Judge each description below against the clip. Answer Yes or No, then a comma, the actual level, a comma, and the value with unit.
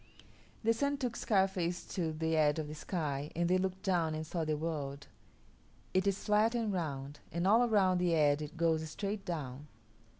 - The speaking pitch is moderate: Yes, medium, 170 Hz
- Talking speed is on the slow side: No, average, 190 wpm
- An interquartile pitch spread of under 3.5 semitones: No, average, 4.0 semitones